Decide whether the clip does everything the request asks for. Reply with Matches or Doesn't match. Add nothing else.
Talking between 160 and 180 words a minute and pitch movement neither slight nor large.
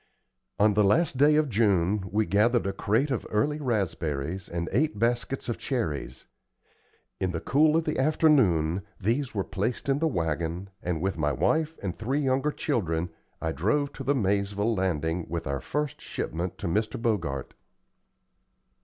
Doesn't match